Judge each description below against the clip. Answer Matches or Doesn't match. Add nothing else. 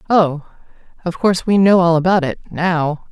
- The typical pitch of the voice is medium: Matches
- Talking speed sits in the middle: Matches